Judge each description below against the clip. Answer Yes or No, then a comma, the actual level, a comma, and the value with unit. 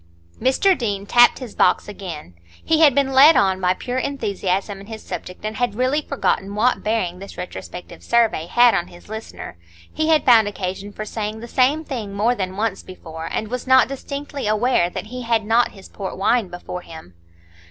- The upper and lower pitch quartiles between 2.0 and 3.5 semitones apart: No, average, 4.6 semitones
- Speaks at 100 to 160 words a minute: No, average, 195 wpm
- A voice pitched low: No, high, 220 Hz